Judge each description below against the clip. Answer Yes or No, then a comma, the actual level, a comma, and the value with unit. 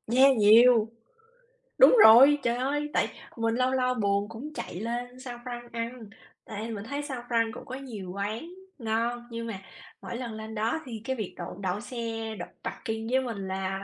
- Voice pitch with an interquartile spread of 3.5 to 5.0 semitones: No, average, 2.7 semitones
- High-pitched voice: Yes, high, 230 Hz